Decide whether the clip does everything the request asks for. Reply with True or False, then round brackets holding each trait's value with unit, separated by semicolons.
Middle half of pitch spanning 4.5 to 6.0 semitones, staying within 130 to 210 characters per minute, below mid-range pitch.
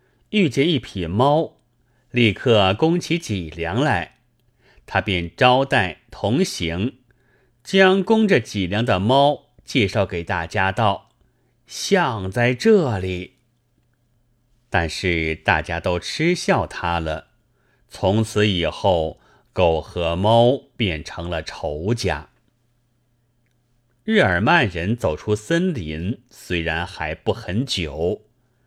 True (5.3 semitones; 145 characters per minute; 115 Hz)